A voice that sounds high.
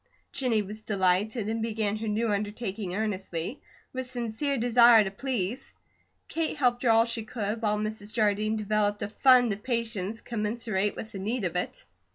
Yes: high, 220 Hz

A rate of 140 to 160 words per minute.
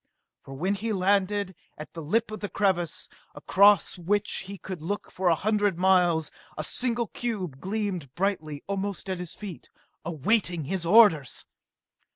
Yes: average, 155 wpm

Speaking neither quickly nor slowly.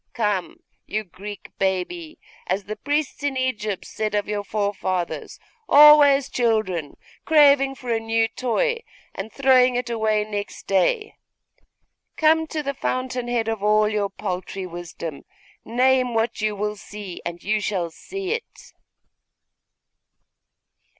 No: slow, 130 wpm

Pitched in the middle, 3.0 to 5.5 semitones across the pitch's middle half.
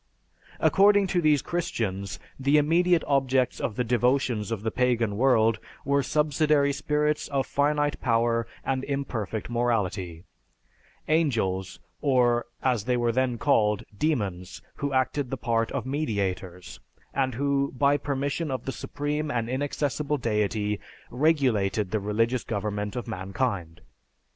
No: low, 125 Hz; average, 4.8 semitones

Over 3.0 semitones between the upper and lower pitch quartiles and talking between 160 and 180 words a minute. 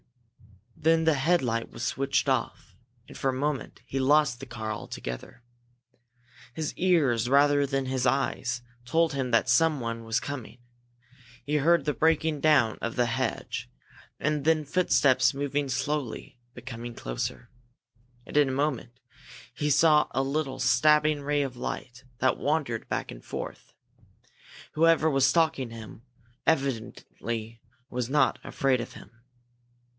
No: average, 3.8 semitones; average, 140 wpm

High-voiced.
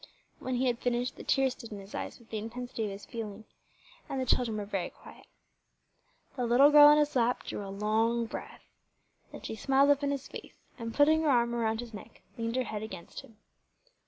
Yes: high, 235 Hz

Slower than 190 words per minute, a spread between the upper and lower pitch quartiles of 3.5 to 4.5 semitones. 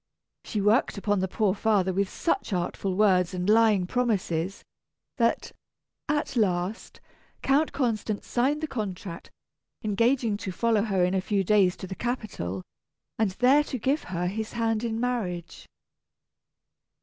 Yes: average, 145 wpm; average, 3.9 semitones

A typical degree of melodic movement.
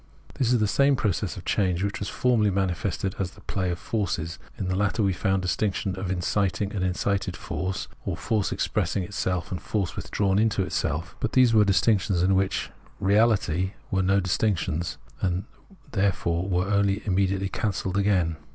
No: narrow, 2.0 semitones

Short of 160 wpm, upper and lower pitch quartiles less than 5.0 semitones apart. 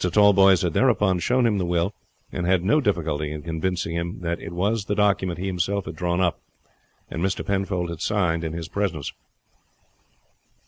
No: average, 180 wpm; average, 2.9 semitones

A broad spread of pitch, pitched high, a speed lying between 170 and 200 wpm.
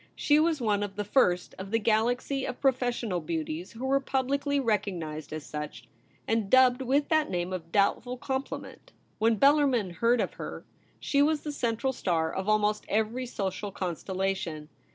Yes: wide, 5.9 semitones; high, 220 Hz; average, 175 wpm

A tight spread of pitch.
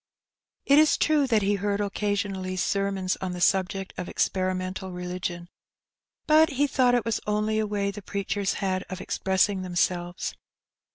Yes: narrow, 2.2 semitones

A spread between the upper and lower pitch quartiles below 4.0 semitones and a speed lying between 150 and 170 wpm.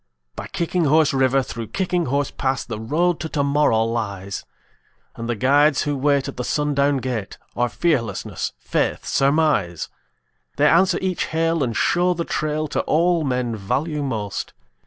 No: average, 5.0 semitones; average, 155 wpm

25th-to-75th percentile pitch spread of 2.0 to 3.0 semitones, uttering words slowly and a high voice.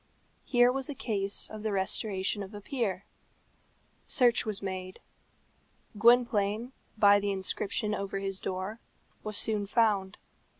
Yes: narrow, 2.4 semitones; slow, 130 wpm; high, 205 Hz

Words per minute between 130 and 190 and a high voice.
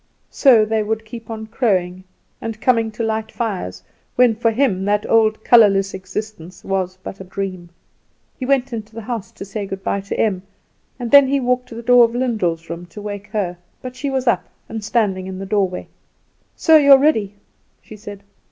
No: average, 200 wpm; high, 215 Hz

